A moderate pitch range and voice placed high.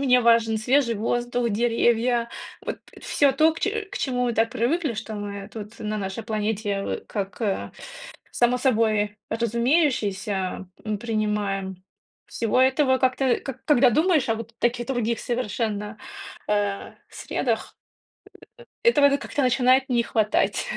Yes: average, 3.4 semitones; high, 230 Hz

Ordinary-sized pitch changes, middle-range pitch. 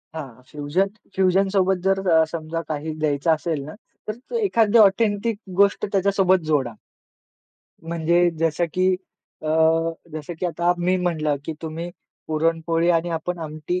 Yes: average, 3.4 semitones; medium, 170 Hz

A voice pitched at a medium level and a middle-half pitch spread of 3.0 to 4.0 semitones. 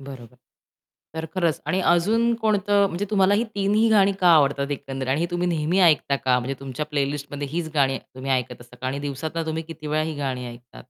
No: medium, 150 Hz; average, 4.9 semitones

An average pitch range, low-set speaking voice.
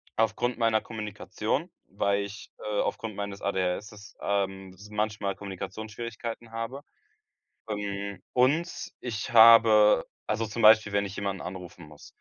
No: narrow, 2.1 semitones; low, 105 Hz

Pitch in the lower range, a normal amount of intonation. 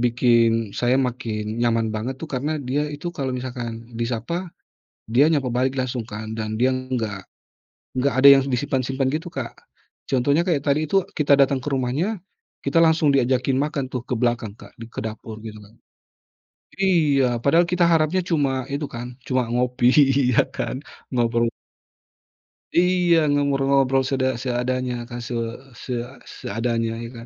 Yes: low, 130 Hz; average, 3.1 semitones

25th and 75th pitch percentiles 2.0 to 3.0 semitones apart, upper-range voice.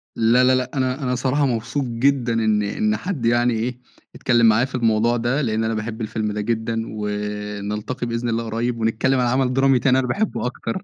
No: narrow, 2.5 semitones; low, 120 Hz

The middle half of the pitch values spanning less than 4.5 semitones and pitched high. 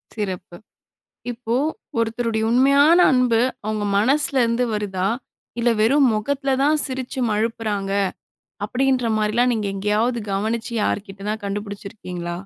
Yes: average, 3.3 semitones; high, 225 Hz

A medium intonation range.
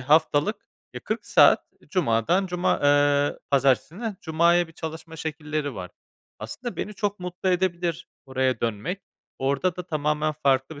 Yes: average, 4.0 semitones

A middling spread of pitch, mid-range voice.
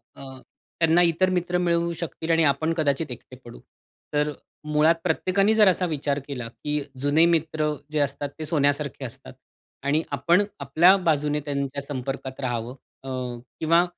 Yes: average, 3.2 semitones; medium, 150 Hz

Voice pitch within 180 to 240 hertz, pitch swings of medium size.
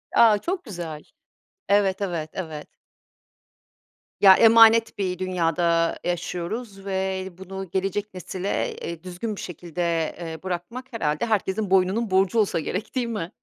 Yes: high, 190 Hz; average, 3.2 semitones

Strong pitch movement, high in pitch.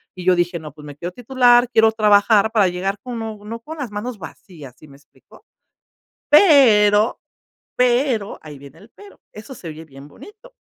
Yes: wide, 6.1 semitones; high, 210 Hz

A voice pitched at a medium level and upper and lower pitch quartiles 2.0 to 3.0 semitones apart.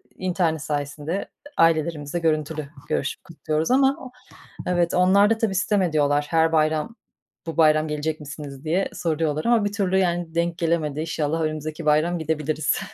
Yes: medium, 160 Hz; narrow, 2.4 semitones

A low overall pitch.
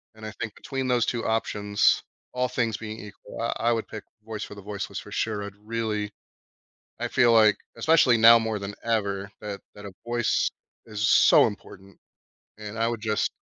Yes: low, 110 Hz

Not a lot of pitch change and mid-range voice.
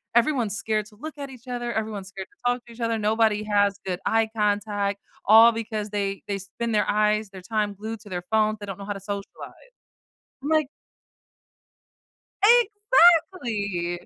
No: narrow, 2.2 semitones; high, 215 Hz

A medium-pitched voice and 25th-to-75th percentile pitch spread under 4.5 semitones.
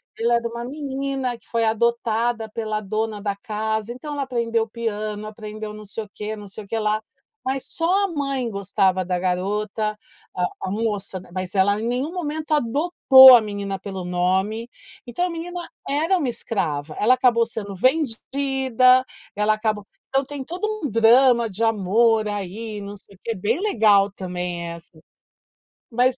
No: high, 225 Hz; average, 4.0 semitones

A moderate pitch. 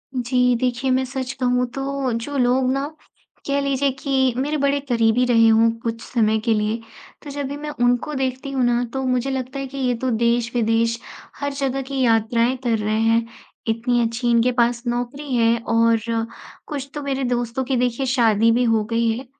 No: high, 245 Hz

